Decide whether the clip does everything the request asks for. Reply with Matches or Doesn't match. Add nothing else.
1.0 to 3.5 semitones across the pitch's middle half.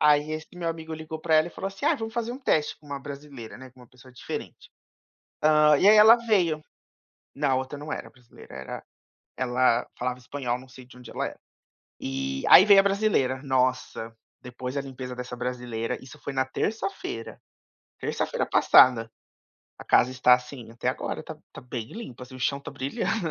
Doesn't match